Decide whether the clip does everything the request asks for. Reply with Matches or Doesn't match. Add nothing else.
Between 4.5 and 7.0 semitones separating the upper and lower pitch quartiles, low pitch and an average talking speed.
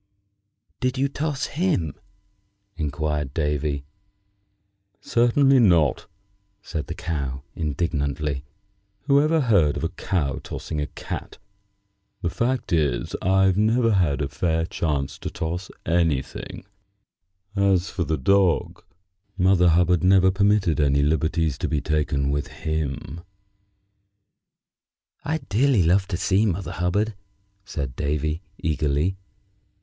Doesn't match